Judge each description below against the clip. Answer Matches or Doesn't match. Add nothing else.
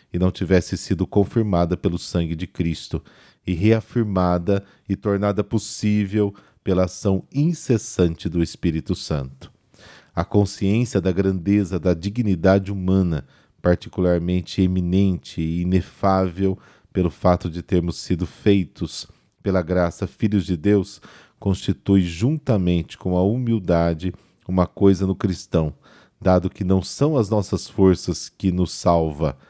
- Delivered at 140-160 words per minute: Doesn't match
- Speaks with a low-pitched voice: Matches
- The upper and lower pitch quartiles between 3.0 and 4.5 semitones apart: Doesn't match